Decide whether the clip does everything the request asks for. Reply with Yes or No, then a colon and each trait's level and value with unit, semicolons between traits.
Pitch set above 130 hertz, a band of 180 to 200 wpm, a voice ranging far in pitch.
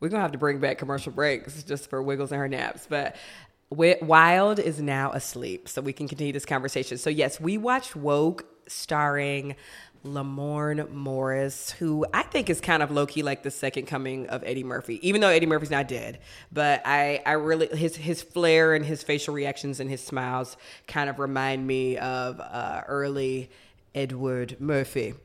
No: medium, 140 Hz; average, 185 wpm; narrow, 2.5 semitones